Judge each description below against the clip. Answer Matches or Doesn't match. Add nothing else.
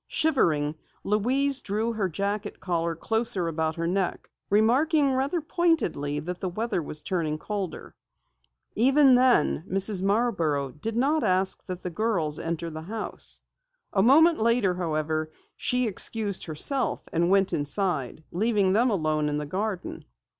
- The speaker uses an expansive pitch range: Matches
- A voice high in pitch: Matches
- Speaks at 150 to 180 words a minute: Doesn't match